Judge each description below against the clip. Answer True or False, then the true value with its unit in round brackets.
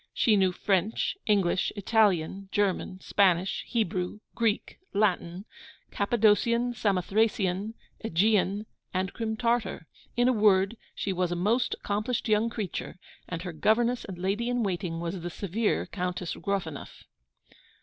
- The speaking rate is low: True (130 wpm)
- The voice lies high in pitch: True (200 Hz)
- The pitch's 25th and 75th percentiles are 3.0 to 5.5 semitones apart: True (3.4 semitones)